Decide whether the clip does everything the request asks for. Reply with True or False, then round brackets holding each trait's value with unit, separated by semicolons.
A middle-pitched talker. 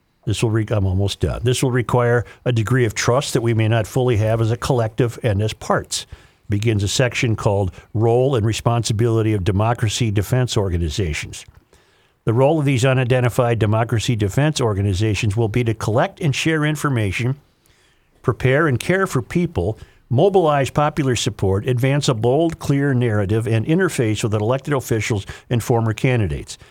False (120 Hz)